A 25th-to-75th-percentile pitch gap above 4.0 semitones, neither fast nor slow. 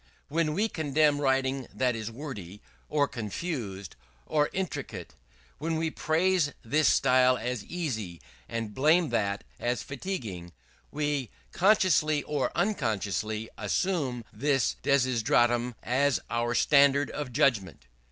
No: average, 5.0 semitones; slow, 115 wpm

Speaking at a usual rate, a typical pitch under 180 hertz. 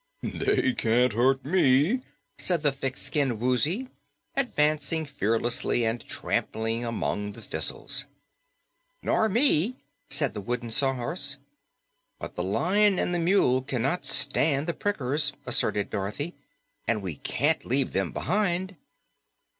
No: slow, 120 wpm; medium, 140 Hz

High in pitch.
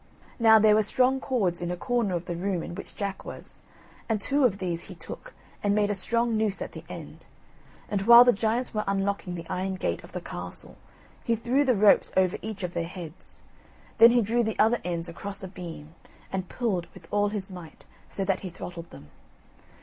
Yes: high, 200 Hz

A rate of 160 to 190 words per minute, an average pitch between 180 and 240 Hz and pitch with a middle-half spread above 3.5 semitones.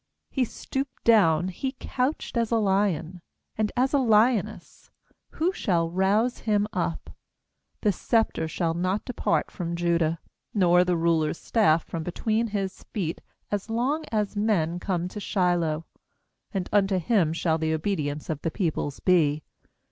No: average, 150 wpm; medium, 185 Hz; average, 4.6 semitones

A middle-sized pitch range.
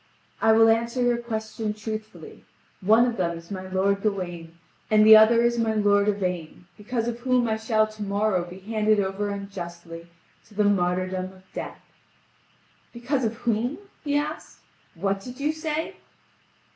Yes: average, 3.6 semitones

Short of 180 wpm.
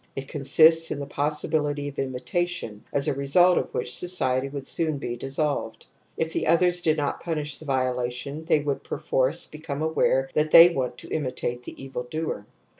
No: average, 185 wpm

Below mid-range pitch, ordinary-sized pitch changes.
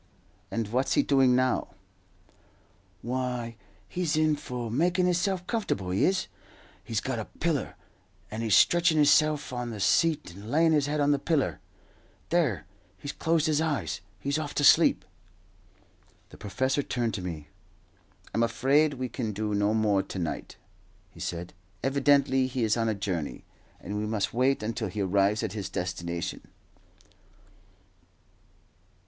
No: low, 125 Hz; wide, 6.0 semitones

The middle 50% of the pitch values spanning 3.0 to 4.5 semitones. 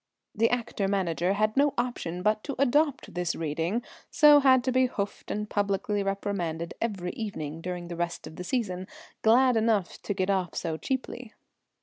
No: average, 5.3 semitones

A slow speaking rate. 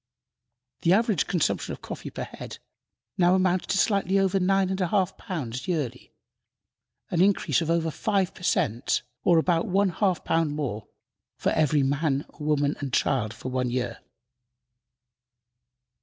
No: average, 150 wpm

